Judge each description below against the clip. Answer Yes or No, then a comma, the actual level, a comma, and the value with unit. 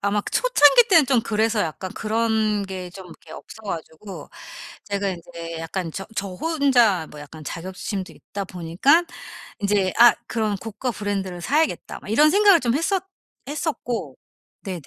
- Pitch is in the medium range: No, high, 205 Hz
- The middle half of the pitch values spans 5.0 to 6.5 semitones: Yes, average, 5.3 semitones